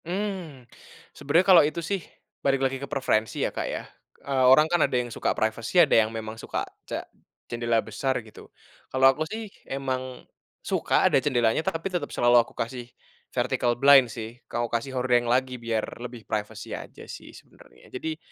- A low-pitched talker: Yes, low, 130 Hz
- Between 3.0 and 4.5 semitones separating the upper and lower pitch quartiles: Yes, average, 3.4 semitones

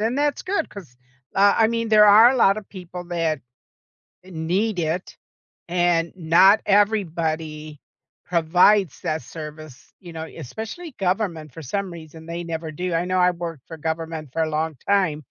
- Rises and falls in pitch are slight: No, average, 4.0 semitones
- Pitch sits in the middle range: Yes, medium, 170 Hz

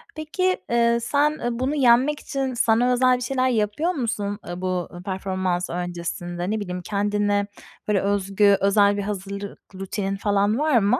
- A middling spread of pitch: Yes, average, 4.2 semitones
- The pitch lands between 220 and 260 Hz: No, high, 205 Hz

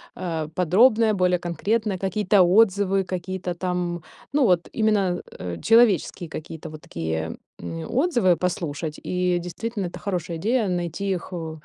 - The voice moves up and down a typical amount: Yes, average, 3.3 semitones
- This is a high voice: No, medium, 180 Hz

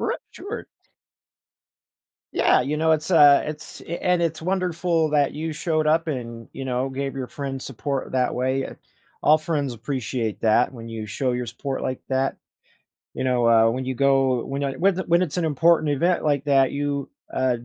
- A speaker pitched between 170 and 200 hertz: No, medium, 140 Hz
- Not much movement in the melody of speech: No, average, 3.5 semitones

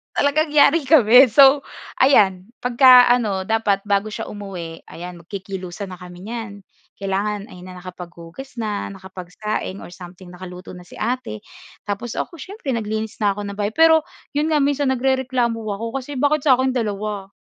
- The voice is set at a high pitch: Yes, high, 215 Hz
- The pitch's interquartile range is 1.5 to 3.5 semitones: No, wide, 5.6 semitones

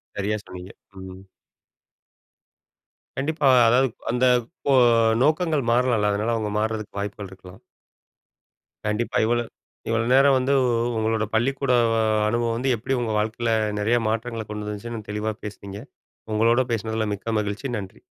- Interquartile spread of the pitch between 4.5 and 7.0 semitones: No, average, 2.8 semitones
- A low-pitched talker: Yes, low, 115 Hz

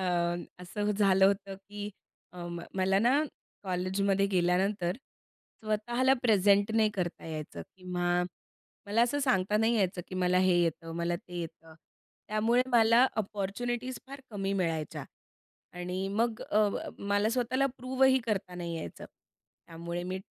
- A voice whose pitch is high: Yes, high, 195 Hz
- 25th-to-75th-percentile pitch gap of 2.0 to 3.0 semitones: No, average, 3.7 semitones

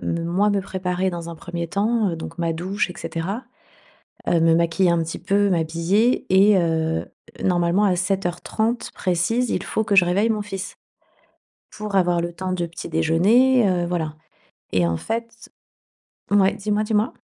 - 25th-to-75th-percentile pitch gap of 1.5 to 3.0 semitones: No, average, 3.5 semitones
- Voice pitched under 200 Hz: Yes, medium, 185 Hz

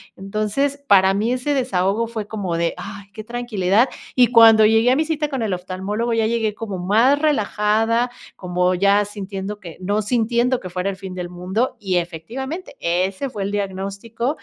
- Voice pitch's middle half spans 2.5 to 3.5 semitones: No, average, 3.9 semitones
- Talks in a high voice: Yes, high, 210 Hz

